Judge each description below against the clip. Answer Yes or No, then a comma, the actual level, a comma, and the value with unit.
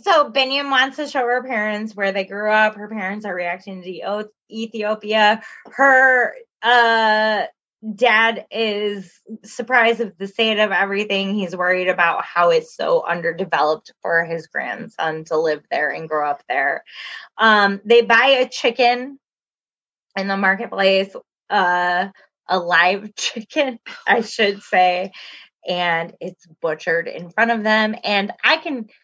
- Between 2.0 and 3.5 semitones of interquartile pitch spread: No, average, 4.4 semitones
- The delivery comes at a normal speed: Yes, average, 145 wpm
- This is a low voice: No, high, 210 Hz